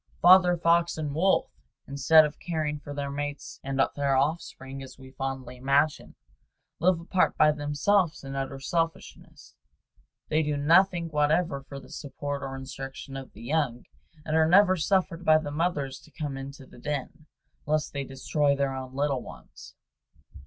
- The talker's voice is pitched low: No, medium, 145 Hz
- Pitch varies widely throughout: No, average, 3.0 semitones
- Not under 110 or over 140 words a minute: No, average, 160 wpm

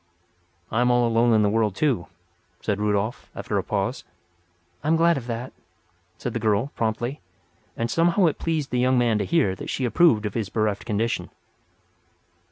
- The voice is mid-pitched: No, low, 115 Hz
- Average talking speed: Yes, average, 180 wpm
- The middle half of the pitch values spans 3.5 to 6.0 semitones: Yes, average, 3.9 semitones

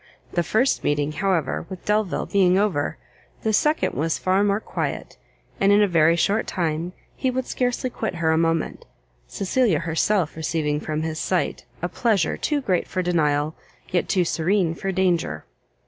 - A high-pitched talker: No, medium, 180 Hz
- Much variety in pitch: No, average, 4.2 semitones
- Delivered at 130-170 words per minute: Yes, average, 165 wpm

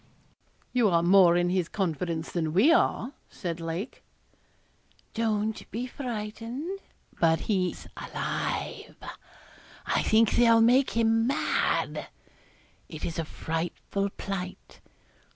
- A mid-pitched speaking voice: No, high, 200 Hz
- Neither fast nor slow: No, slow, 110 wpm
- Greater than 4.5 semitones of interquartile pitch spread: Yes, average, 5.0 semitones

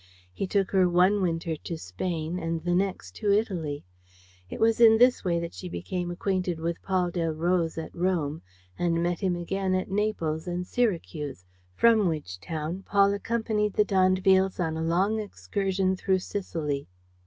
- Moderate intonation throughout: Yes, average, 3.0 semitones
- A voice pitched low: No, medium, 180 Hz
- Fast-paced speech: No, average, 165 wpm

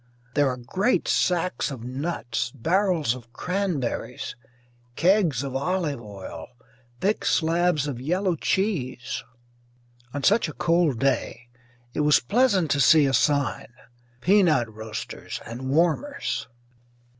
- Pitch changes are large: Yes, wide, 6.1 semitones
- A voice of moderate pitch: Yes, medium, 150 Hz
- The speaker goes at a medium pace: No, slow, 120 wpm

